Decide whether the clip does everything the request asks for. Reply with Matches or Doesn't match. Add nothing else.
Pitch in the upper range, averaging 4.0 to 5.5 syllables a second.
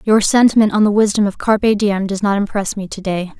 Doesn't match